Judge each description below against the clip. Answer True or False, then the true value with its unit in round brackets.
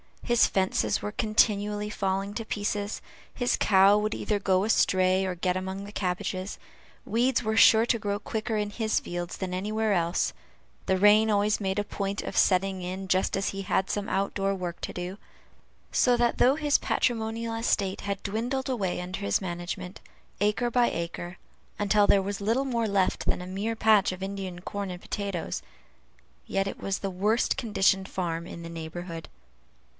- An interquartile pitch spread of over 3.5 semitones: False (2.6 semitones)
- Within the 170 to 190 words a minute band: True (180 wpm)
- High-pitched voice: True (200 Hz)